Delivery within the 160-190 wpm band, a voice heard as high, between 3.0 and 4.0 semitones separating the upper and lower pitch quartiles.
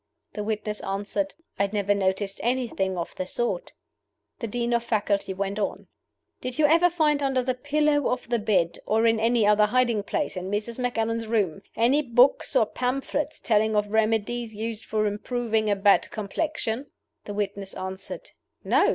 Yes: average, 170 wpm; high, 220 Hz; average, 3.4 semitones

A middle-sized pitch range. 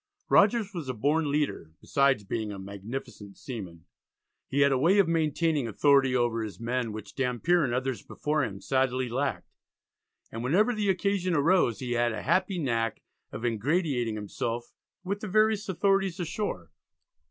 No: wide, 7.1 semitones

